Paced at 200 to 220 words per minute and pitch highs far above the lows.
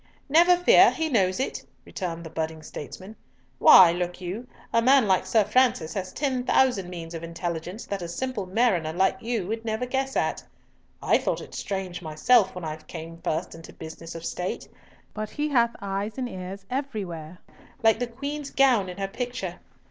No: average, 180 wpm; wide, 6.1 semitones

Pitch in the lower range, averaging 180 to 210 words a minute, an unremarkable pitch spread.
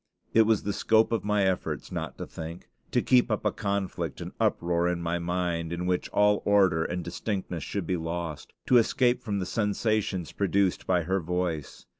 Yes: very low, 95 Hz; average, 190 wpm; average, 3.1 semitones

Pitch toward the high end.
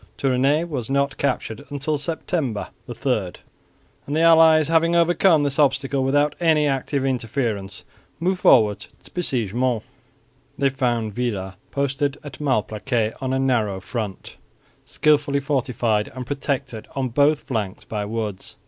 No: low, 135 Hz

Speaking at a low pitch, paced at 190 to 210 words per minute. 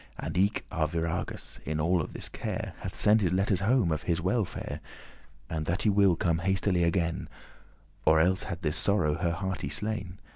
No: very low, 90 Hz; average, 175 wpm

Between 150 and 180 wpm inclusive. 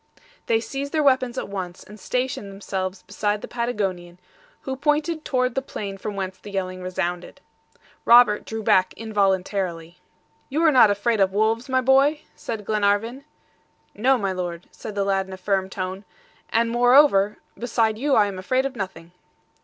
Yes: average, 170 wpm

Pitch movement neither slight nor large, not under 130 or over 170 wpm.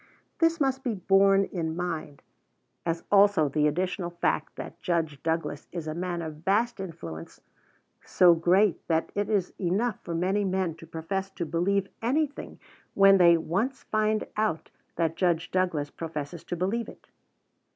Yes: average, 3.4 semitones; average, 155 wpm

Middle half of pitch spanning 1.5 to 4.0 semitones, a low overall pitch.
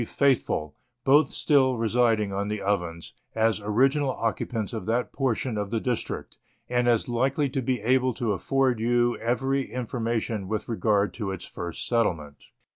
Yes: average, 3.3 semitones; low, 115 Hz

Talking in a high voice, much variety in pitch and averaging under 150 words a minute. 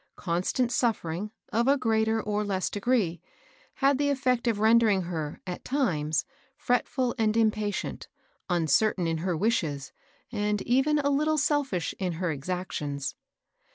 Yes: high, 210 Hz; wide, 6.2 semitones; slow, 135 wpm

